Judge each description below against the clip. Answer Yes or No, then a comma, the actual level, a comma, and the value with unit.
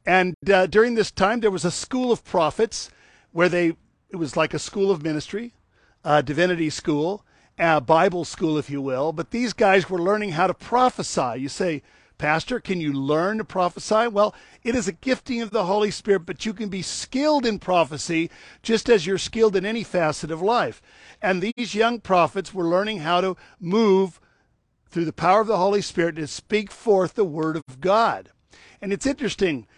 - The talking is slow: No, average, 195 wpm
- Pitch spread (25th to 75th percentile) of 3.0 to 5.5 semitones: Yes, average, 4.3 semitones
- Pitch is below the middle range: No, high, 190 Hz